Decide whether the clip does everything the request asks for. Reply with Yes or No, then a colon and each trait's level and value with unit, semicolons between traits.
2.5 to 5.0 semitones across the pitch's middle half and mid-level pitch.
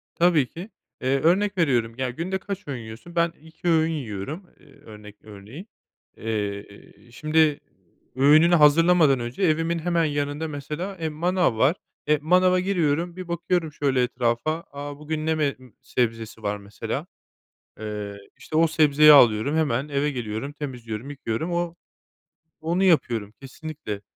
No: wide, 5.6 semitones; medium, 150 Hz